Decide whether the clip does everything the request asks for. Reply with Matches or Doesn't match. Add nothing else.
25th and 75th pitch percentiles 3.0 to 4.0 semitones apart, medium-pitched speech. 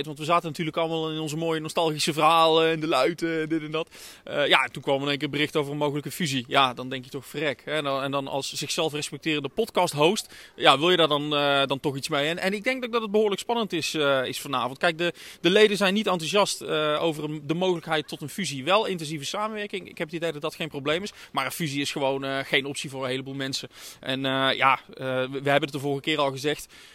Matches